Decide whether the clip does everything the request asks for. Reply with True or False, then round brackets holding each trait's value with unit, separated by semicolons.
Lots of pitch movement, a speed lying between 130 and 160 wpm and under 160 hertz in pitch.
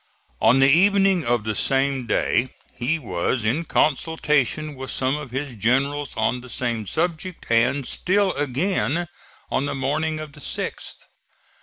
False (4.0 semitones; 150 wpm; 140 Hz)